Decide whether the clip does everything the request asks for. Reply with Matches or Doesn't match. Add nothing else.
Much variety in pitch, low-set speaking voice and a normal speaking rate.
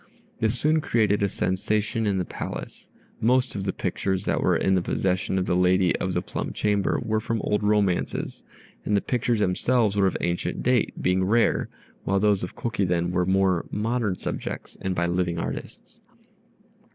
Doesn't match